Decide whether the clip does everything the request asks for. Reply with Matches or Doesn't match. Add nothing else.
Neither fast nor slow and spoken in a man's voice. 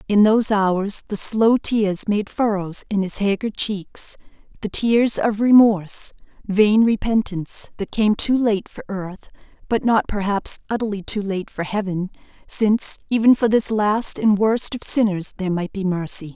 Doesn't match